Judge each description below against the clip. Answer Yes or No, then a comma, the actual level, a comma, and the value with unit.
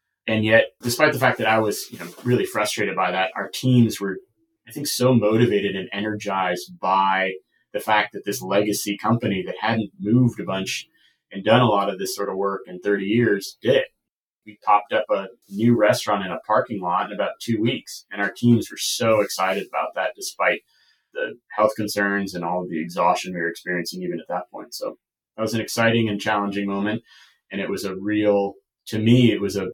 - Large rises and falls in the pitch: No, average, 2.9 semitones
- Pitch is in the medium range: No, low, 105 Hz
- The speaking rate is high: Yes, fast, 210 wpm